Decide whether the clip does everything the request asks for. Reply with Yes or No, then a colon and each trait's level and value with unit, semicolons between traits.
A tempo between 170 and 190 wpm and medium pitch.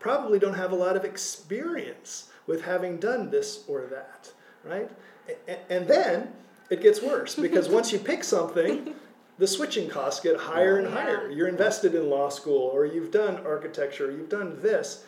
No: average, 175 wpm; high, 205 Hz